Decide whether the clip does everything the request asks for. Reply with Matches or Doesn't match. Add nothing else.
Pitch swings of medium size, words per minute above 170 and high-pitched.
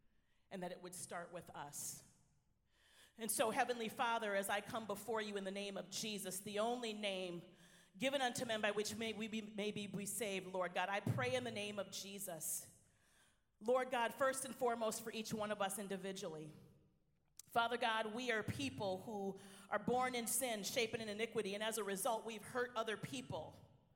Matches